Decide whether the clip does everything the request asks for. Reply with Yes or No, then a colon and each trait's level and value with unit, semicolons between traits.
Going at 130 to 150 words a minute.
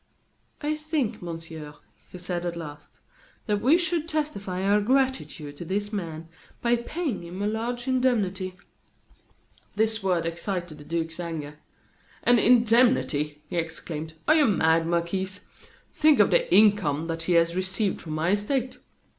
Yes: average, 145 wpm